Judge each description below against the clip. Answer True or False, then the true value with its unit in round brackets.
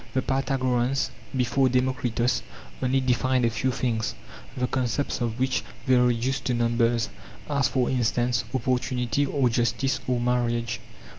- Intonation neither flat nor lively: False (1.7 semitones)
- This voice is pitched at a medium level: False (125 Hz)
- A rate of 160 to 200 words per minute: False (140 wpm)